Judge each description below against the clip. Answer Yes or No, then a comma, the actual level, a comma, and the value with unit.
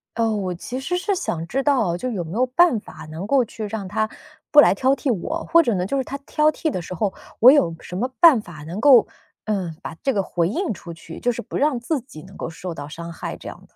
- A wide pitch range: Yes, wide, 7.3 semitones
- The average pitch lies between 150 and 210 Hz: No, high, 220 Hz